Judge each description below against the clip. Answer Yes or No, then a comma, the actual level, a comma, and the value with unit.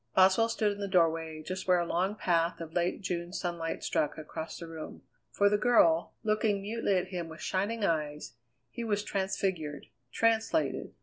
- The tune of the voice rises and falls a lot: No, average, 3.8 semitones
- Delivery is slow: No, average, 175 wpm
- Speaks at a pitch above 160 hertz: Yes, medium, 185 Hz